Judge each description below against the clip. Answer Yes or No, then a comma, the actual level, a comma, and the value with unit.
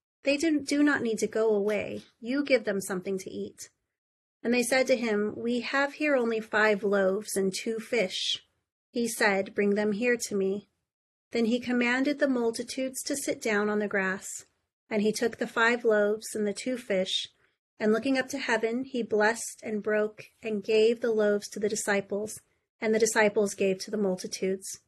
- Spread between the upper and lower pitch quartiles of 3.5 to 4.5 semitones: No, average, 2.8 semitones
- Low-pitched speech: No, high, 220 Hz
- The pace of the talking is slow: No, average, 190 wpm